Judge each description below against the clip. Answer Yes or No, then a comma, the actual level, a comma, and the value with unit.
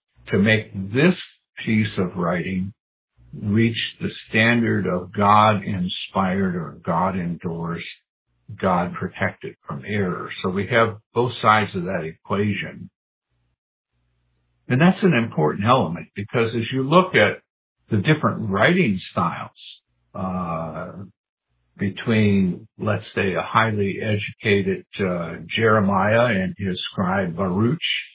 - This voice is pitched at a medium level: No, low, 100 Hz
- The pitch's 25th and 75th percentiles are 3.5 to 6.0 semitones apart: Yes, average, 4.1 semitones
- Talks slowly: Yes, slow, 115 wpm